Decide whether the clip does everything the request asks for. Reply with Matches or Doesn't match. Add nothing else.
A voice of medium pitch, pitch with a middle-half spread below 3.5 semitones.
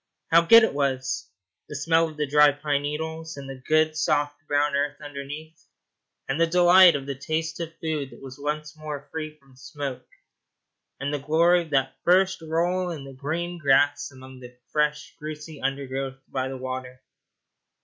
Matches